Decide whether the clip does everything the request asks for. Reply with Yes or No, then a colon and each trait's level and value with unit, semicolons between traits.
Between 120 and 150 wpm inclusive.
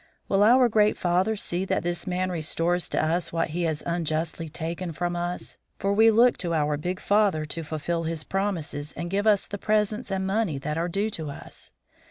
No: fast, 205 wpm